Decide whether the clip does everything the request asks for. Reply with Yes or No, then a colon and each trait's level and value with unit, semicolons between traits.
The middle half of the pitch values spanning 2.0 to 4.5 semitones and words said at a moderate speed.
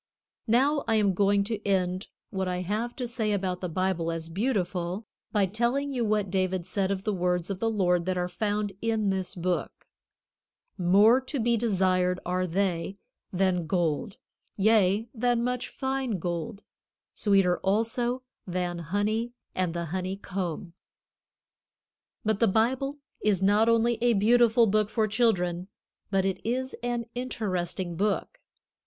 Yes: average, 3.9 semitones; average, 150 wpm